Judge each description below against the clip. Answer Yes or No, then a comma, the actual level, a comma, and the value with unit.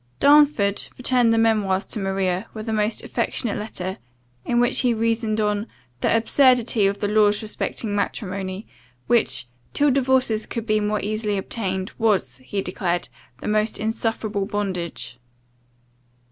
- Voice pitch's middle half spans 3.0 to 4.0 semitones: No, narrow, 2.5 semitones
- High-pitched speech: Yes, high, 215 Hz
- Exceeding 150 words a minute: No, average, 145 wpm